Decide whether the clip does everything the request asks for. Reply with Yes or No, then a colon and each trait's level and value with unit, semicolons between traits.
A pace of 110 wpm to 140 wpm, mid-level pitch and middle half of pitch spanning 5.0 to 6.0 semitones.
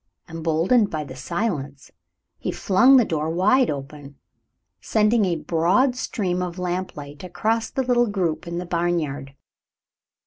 Yes: slow, 135 wpm; medium, 175 Hz; wide, 5.4 semitones